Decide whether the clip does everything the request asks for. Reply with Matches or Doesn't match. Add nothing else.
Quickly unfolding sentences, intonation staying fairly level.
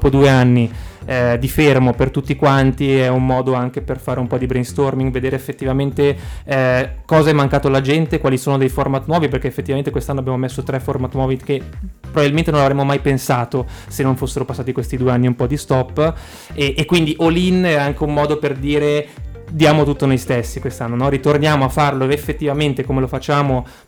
Matches